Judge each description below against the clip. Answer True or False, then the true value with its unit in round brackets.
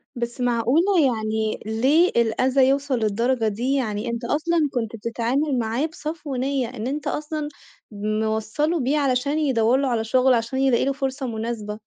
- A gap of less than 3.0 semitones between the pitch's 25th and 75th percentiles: False (3.8 semitones)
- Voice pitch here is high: True (250 Hz)